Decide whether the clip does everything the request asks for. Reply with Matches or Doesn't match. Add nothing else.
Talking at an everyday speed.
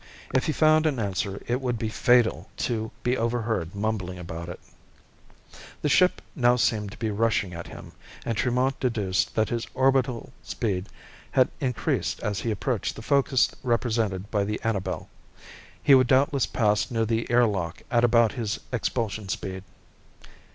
Matches